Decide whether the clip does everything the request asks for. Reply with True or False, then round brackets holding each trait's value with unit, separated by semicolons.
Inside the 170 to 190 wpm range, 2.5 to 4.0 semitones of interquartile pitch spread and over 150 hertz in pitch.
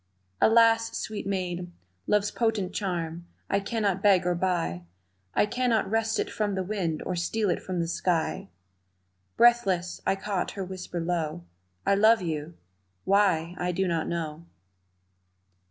False (150 wpm; 3.5 semitones; 185 Hz)